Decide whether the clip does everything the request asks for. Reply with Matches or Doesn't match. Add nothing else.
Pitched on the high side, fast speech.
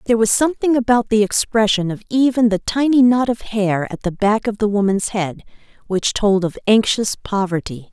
Doesn't match